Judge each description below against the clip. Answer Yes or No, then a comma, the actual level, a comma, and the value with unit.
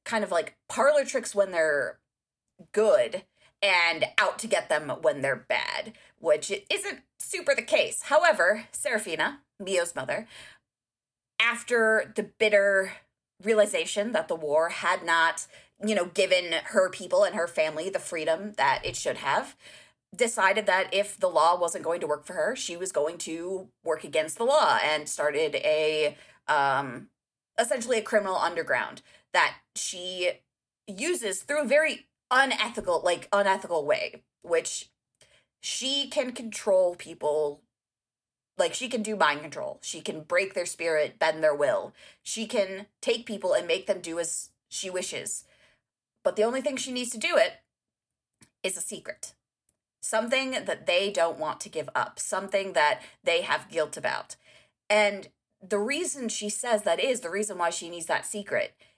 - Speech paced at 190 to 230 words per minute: No, average, 160 wpm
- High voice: Yes, high, 205 Hz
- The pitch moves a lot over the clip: Yes, wide, 6.3 semitones